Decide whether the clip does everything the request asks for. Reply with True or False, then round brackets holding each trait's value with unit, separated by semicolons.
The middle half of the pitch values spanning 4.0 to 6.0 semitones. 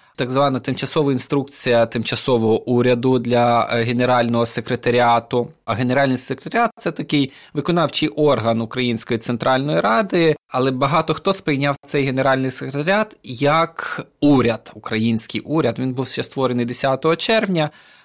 False (3.2 semitones)